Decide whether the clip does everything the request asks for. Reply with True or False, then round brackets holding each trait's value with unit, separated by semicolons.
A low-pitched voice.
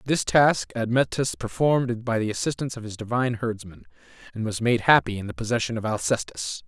True (120 Hz)